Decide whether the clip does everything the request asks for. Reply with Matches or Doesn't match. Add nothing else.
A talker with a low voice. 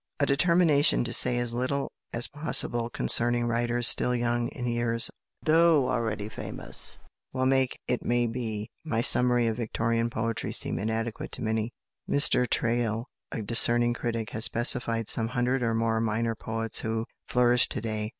Matches